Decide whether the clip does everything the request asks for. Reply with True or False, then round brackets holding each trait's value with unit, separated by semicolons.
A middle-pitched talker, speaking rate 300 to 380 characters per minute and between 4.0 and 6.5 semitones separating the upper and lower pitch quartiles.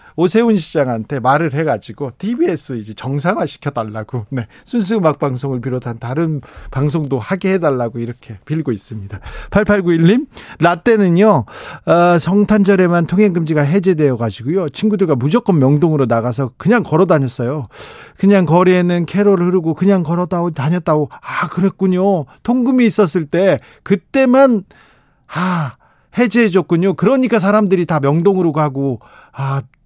True (170 Hz; 325 characters per minute; 6.2 semitones)